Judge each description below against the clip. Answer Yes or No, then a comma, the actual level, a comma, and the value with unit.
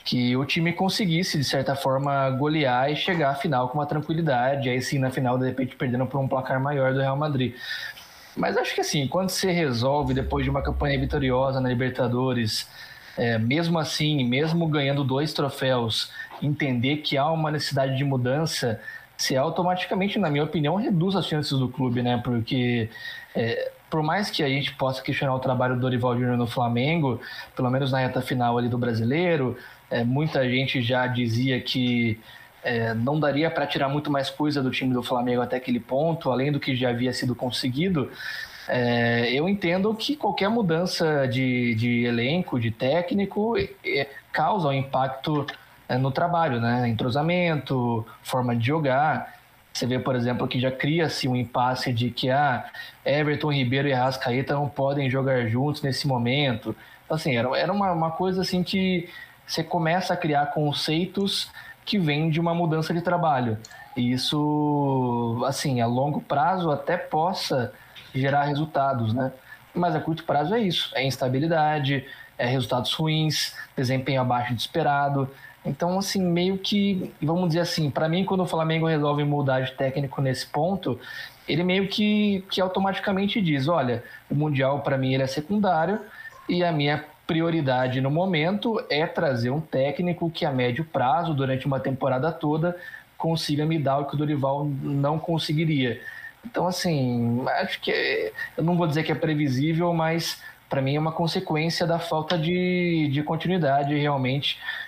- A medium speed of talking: Yes, average, 170 wpm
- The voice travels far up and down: No, average, 4.5 semitones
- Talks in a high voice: No, medium, 145 Hz